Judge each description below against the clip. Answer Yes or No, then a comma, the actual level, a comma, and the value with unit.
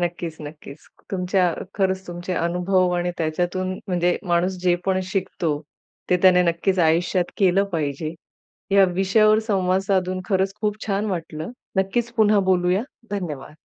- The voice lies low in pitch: No, medium, 180 Hz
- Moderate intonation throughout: No, narrow, 1.9 semitones